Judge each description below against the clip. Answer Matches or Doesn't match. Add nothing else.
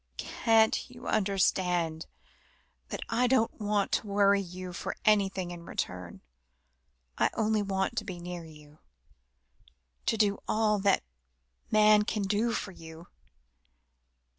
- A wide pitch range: Doesn't match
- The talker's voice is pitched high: Matches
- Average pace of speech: Doesn't match